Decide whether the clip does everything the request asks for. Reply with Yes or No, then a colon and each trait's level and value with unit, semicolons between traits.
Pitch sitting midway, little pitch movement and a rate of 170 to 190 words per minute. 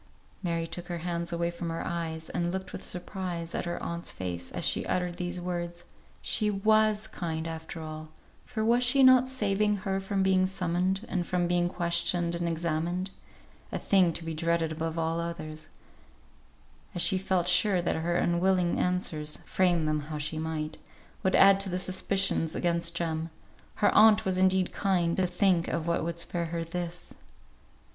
Yes: medium, 175 Hz; narrow, 2.2 semitones; average, 175 wpm